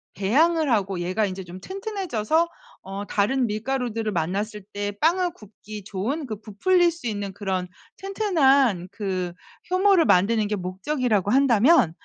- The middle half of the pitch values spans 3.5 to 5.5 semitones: No, wide, 7.5 semitones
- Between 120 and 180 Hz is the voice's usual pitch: No, high, 215 Hz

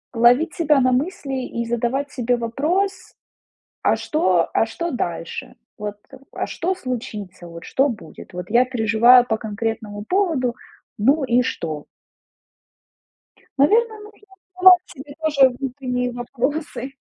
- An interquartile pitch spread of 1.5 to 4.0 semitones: No, average, 4.7 semitones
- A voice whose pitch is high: Yes, very high, 250 Hz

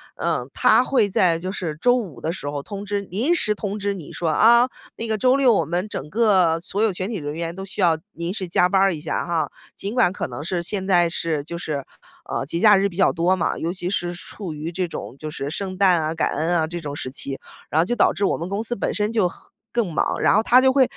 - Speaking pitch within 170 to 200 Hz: Yes, medium, 185 Hz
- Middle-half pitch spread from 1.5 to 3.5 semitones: No, average, 4.0 semitones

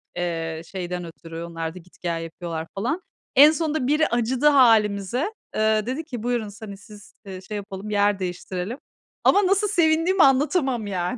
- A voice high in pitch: Yes, high, 215 Hz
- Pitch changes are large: Yes, wide, 7.3 semitones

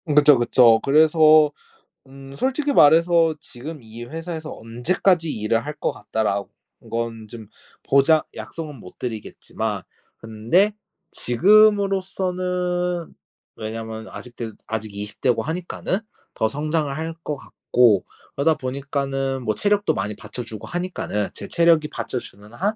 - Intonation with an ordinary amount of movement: No, wide, 6.8 semitones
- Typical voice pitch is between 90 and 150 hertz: Yes, medium, 140 Hz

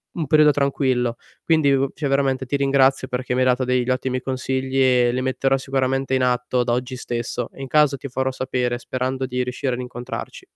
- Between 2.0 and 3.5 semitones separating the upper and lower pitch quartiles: No, narrow, 1.3 semitones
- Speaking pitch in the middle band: No, low, 130 Hz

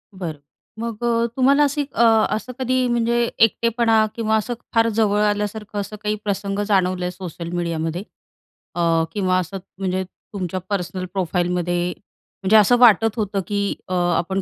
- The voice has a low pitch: No, high, 205 Hz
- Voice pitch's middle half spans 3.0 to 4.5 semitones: Yes, average, 3.7 semitones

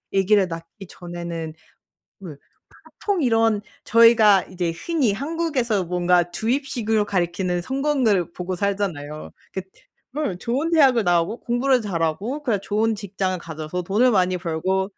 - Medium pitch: No, high, 200 Hz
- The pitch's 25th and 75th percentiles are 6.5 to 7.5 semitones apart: No, average, 5.1 semitones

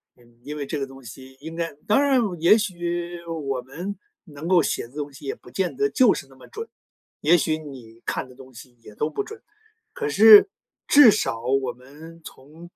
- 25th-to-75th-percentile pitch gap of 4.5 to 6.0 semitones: Yes, average, 5.0 semitones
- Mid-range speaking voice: Yes, medium, 155 Hz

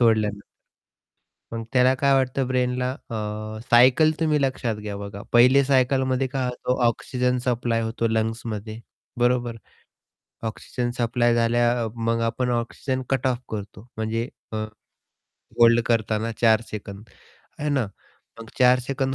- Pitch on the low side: Yes, low, 120 Hz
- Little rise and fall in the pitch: Yes, narrow, 2.2 semitones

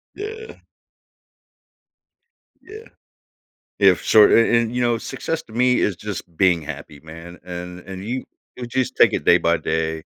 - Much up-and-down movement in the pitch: Yes, wide, 6.1 semitones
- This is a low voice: Yes, low, 100 Hz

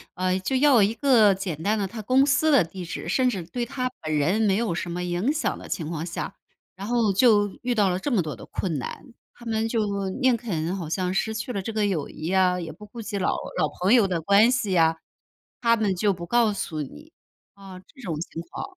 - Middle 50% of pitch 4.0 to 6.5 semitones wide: Yes, average, 4.7 semitones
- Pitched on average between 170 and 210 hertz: Yes, high, 200 Hz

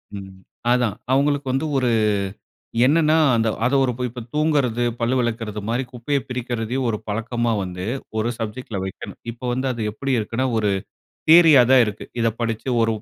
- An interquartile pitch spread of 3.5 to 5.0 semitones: No, average, 2.9 semitones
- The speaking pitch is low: Yes, low, 120 Hz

